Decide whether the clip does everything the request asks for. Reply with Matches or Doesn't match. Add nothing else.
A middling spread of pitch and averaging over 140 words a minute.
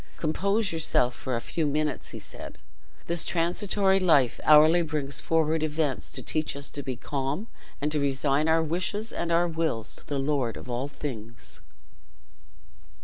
Matches